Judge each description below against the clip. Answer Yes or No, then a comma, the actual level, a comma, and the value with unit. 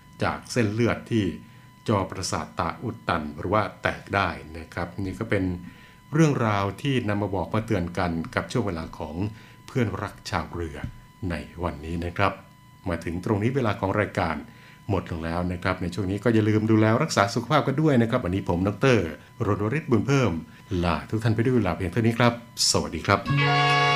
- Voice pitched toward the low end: Yes, low, 105 Hz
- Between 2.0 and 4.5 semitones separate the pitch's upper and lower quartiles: No, average, 5.1 semitones